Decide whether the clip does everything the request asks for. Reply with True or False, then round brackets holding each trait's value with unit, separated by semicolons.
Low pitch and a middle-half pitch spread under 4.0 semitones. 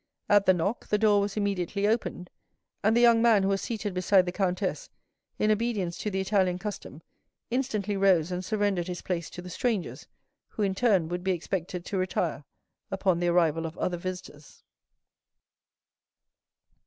False (190 Hz; 2.8 semitones)